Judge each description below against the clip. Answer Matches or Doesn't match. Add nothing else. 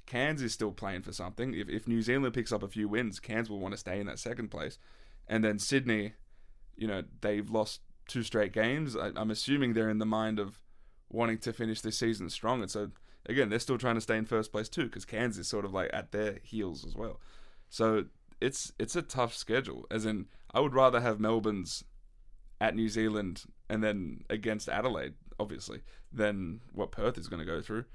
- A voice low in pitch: Matches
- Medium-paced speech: Doesn't match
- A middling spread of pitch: Doesn't match